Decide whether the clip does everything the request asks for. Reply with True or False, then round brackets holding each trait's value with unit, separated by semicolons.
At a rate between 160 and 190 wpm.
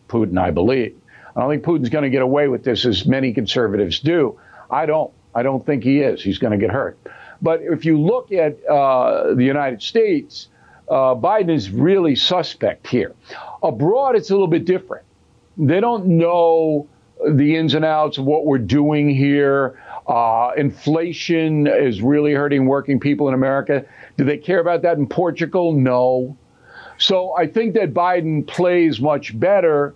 True (175 wpm)